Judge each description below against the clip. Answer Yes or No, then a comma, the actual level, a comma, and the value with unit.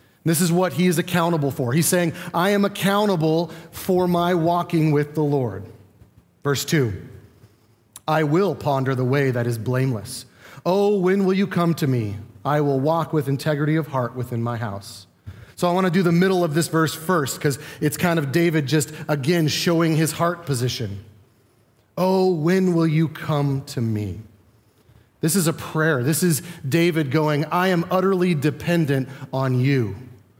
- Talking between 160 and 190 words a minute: Yes, average, 175 wpm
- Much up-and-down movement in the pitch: Yes, wide, 5.7 semitones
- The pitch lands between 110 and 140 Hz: No, medium, 155 Hz